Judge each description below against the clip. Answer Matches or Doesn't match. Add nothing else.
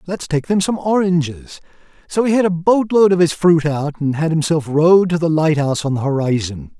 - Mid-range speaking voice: Matches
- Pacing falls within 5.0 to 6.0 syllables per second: Matches